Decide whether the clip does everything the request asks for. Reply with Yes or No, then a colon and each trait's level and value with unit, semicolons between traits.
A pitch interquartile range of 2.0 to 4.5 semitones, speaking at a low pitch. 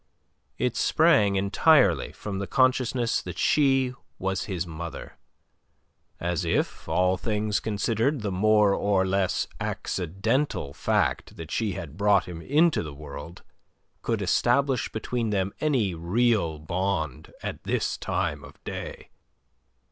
No: average, 4.9 semitones; low, 100 Hz